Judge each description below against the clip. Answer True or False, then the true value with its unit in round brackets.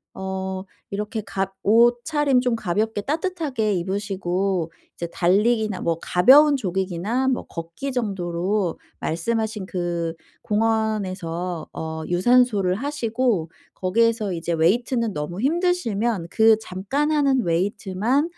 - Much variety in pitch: False (4.9 semitones)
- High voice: True (205 Hz)